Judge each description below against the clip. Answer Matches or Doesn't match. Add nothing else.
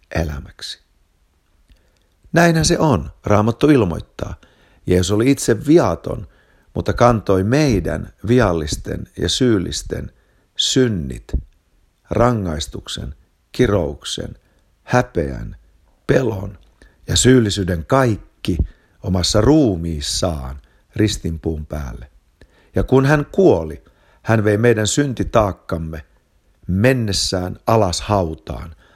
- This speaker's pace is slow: Matches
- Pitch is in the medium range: Doesn't match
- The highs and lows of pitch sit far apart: Matches